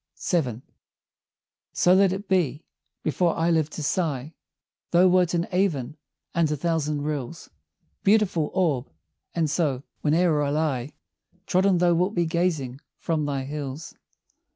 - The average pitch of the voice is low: No, medium, 160 Hz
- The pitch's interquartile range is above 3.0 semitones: Yes, average, 3.5 semitones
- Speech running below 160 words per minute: Yes, slow, 135 wpm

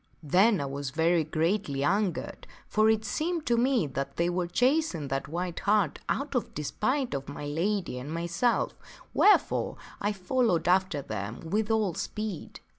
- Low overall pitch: No, medium, 180 Hz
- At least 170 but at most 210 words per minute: No, average, 160 wpm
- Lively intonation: Yes, wide, 6.4 semitones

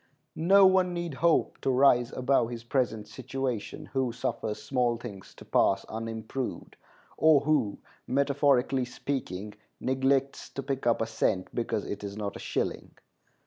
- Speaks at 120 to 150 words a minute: Yes, average, 145 wpm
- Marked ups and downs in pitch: No, average, 3.5 semitones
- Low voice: Yes, low, 125 Hz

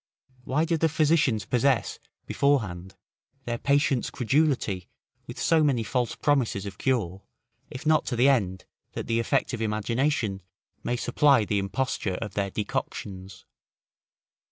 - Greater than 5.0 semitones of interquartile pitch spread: Yes, wide, 5.6 semitones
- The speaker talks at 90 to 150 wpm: Yes, average, 140 wpm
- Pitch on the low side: Yes, low, 120 Hz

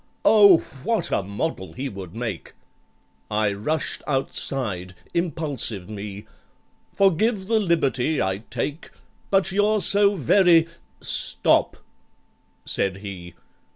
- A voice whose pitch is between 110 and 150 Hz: Yes, medium, 140 Hz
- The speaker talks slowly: Yes, slow, 95 wpm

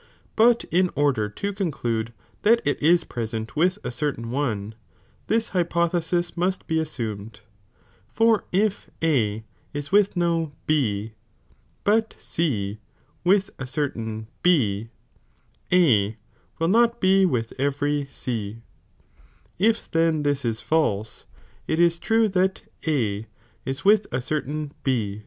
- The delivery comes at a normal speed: No, slow, 130 wpm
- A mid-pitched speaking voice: Yes, medium, 150 Hz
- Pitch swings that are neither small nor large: No, wide, 7.9 semitones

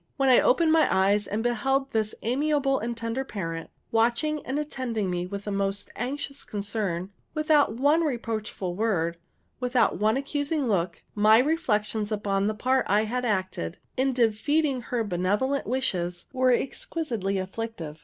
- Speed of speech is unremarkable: Yes, average, 150 wpm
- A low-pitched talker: No, high, 225 Hz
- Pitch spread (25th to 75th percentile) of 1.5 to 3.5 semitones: No, average, 5.0 semitones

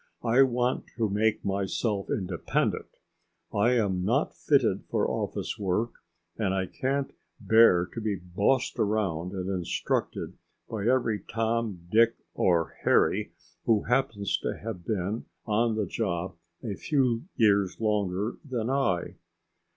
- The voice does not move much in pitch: No, average, 3.5 semitones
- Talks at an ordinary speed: No, slow, 130 wpm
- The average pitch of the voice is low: Yes, low, 105 Hz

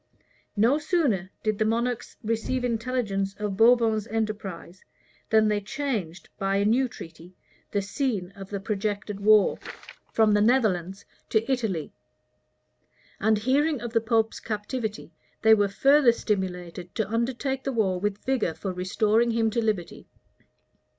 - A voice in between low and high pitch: No, high, 215 Hz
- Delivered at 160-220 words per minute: No, average, 140 wpm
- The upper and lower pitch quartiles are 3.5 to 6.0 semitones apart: No, average, 3.1 semitones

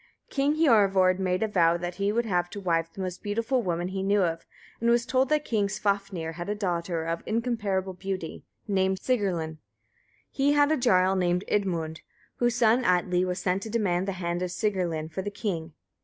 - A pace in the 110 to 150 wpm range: No, average, 195 wpm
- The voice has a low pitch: No, high, 190 Hz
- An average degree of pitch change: Yes, average, 3.7 semitones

